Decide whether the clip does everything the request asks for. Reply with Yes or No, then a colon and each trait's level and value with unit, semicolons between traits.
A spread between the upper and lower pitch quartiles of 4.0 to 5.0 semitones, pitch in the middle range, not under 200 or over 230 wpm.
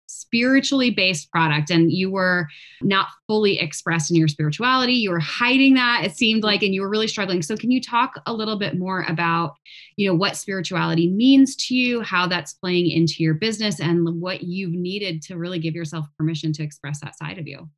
Yes: average, 4.7 semitones; medium, 180 Hz; fast, 205 wpm